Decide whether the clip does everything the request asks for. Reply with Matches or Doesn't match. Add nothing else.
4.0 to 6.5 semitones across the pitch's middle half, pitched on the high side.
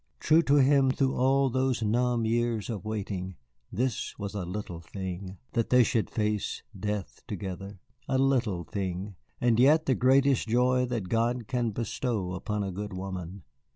Doesn't match